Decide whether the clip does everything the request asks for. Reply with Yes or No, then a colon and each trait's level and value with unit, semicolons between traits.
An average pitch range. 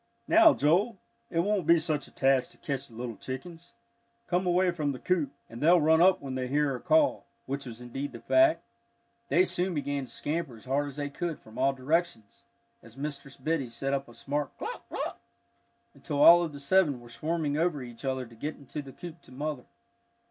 Yes: average, 4.4 semitones